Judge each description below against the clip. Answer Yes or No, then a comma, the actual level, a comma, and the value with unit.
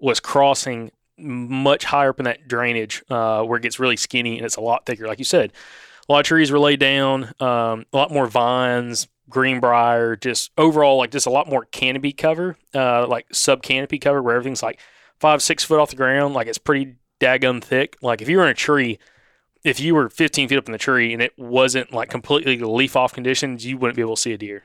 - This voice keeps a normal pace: No, fast, 235 wpm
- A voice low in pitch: Yes, low, 130 Hz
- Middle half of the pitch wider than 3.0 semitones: No, average, 2.7 semitones